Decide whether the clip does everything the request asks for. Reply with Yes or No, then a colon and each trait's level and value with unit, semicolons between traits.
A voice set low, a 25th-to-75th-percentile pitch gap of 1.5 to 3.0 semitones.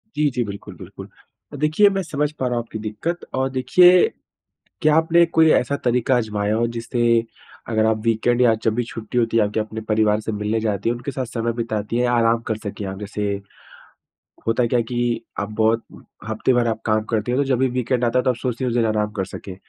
Yes: low, 115 Hz; average, 2.7 semitones